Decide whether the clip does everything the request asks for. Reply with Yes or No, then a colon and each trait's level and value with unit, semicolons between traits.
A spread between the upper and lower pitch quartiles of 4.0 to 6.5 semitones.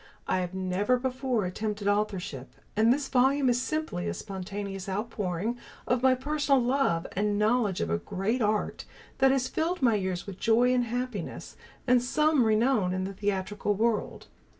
Yes: average, 4.6 semitones